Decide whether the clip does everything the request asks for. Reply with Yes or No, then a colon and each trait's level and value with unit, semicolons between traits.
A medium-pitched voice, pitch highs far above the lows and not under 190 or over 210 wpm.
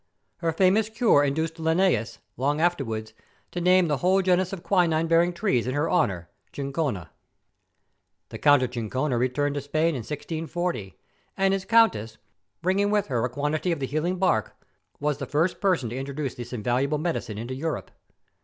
No: medium, 150 Hz; wide, 5.7 semitones; average, 170 wpm